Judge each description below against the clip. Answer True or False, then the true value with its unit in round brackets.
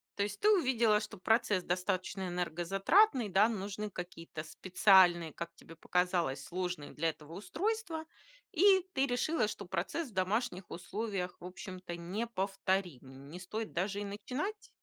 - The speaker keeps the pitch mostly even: False (4.2 semitones)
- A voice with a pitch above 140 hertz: True (190 Hz)